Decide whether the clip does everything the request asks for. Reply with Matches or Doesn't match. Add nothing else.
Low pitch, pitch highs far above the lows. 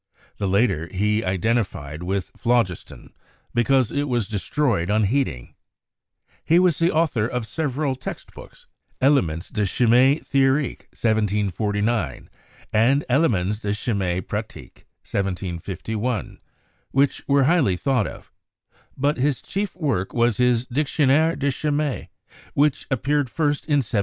Matches